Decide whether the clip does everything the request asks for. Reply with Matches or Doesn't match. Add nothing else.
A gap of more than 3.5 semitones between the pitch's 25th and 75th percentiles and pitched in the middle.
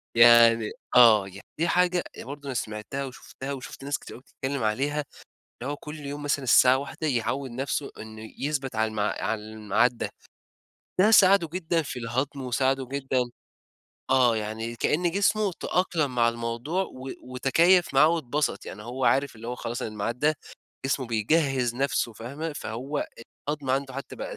Doesn't match